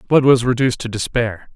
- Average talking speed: Yes, average, 195 wpm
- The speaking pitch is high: No, low, 120 Hz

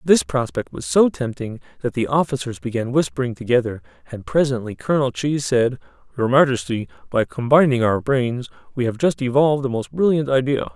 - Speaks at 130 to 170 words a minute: Yes, average, 165 wpm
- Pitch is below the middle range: Yes, low, 125 Hz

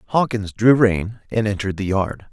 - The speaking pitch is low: Yes, low, 105 Hz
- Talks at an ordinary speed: Yes, average, 180 wpm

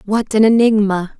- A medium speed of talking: Yes, average, 150 wpm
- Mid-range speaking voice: No, high, 210 Hz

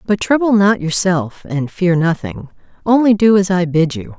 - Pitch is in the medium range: Yes, medium, 180 Hz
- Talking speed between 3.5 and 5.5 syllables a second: Yes, 4.6 syllables/s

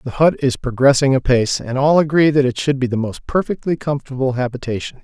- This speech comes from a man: Yes, male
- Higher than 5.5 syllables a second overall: Yes, 6.1 syllables/s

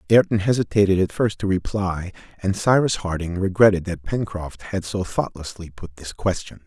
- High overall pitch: No, very low, 95 Hz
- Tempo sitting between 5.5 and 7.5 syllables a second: No, 5.1 syllables/s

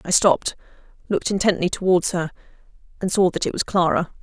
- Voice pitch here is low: No, medium, 185 Hz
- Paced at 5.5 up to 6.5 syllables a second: Yes, 6.3 syllables/s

